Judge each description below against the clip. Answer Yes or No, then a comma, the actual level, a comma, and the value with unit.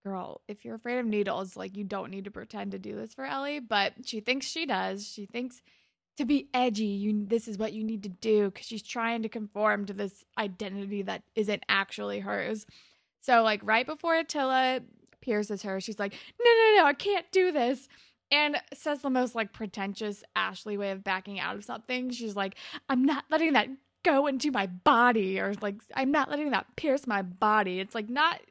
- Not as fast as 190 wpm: No, fast, 205 wpm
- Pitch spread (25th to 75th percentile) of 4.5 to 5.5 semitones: Yes, average, 4.9 semitones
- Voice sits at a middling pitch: No, high, 225 Hz